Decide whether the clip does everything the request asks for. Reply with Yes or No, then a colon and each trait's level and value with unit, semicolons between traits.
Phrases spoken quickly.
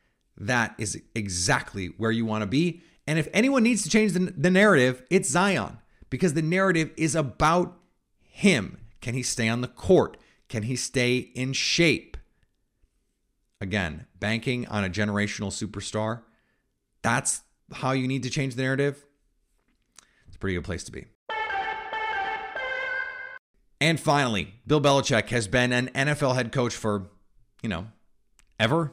No: average, 145 wpm